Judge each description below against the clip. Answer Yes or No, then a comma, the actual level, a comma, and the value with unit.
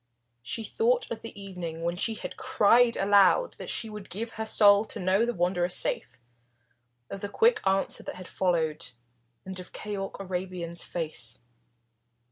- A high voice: Yes, high, 195 Hz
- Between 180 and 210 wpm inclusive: No, average, 160 wpm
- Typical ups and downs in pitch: Yes, average, 3.8 semitones